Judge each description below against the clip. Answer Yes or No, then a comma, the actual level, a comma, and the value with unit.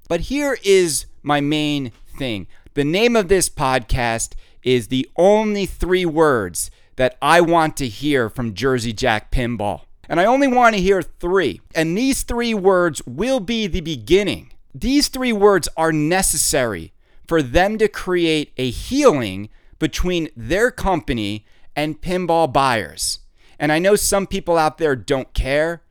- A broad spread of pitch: Yes, wide, 7.2 semitones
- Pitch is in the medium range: Yes, medium, 155 Hz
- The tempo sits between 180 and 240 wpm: No, average, 155 wpm